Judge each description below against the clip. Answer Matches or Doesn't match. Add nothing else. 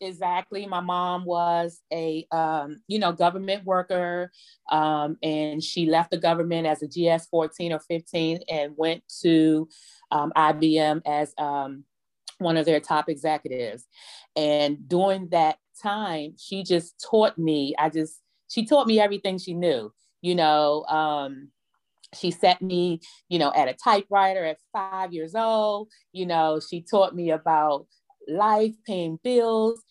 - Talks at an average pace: Matches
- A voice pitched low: Doesn't match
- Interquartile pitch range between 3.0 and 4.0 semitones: Matches